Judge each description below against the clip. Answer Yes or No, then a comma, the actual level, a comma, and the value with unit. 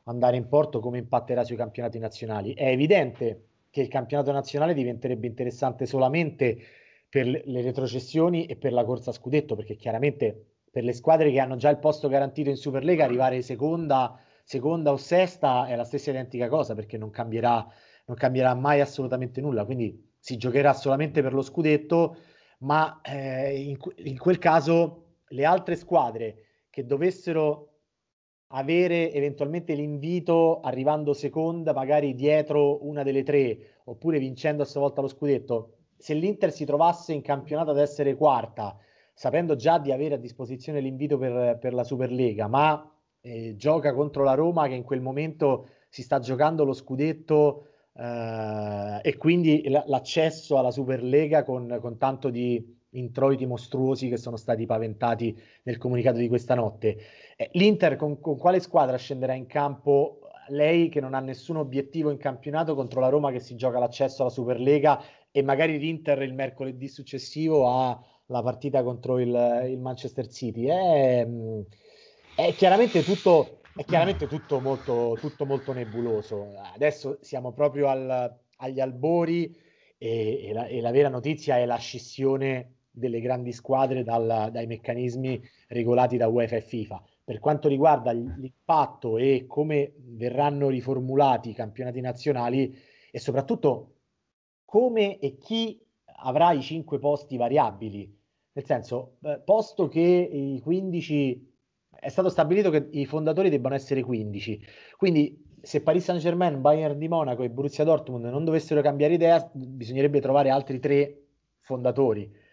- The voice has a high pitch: No, low, 135 Hz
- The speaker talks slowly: No, average, 150 wpm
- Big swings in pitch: No, average, 3.4 semitones